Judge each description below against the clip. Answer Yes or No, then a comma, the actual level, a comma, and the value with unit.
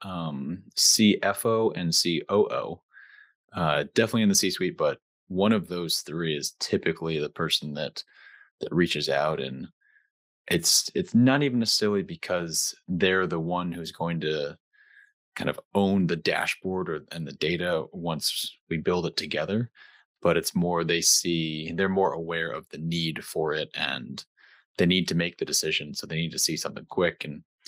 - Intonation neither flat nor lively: Yes, average, 3.9 semitones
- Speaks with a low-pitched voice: Yes, very low, 90 Hz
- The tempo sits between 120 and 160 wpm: No, average, 180 wpm